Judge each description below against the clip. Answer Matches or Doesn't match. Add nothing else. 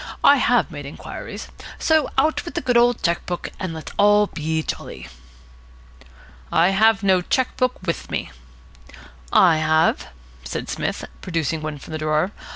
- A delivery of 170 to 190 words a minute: Doesn't match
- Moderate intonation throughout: Doesn't match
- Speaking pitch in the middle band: Matches